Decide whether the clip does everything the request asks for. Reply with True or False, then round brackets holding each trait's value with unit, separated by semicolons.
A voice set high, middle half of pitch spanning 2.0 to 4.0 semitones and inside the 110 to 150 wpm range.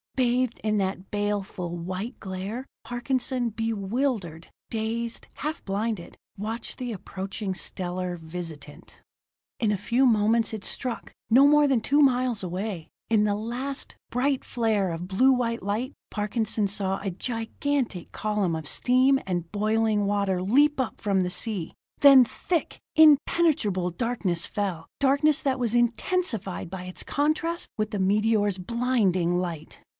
False (215 Hz; 4.8 semitones; 140 wpm)